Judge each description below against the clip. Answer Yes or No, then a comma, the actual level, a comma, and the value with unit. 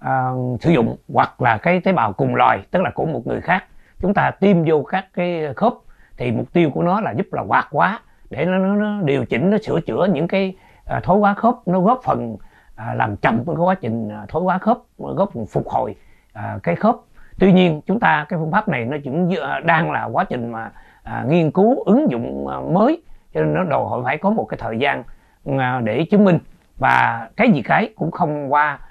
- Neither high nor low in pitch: Yes, medium, 170 Hz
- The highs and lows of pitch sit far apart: Yes, wide, 6.7 semitones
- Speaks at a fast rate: No, average, 215 wpm